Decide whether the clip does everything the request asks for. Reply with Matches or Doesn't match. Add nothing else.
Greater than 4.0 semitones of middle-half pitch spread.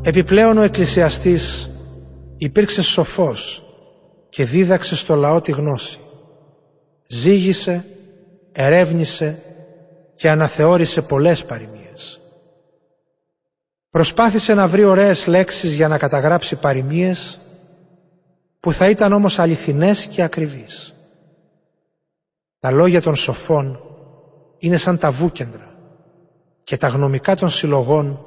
Doesn't match